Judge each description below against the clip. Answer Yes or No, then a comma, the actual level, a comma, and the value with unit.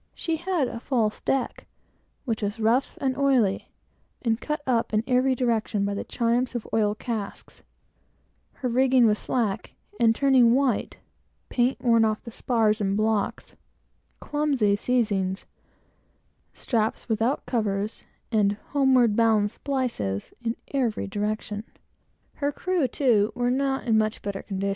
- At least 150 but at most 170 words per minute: No, average, 140 wpm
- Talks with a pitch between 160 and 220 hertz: No, high, 230 Hz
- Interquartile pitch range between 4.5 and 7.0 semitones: No, average, 3.5 semitones